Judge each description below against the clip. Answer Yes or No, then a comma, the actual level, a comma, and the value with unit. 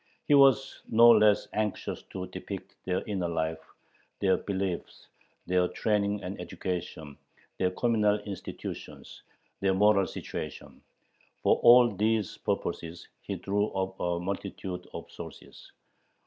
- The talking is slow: Yes, slow, 120 wpm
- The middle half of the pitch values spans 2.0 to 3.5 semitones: Yes, average, 2.8 semitones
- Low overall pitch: Yes, low, 100 Hz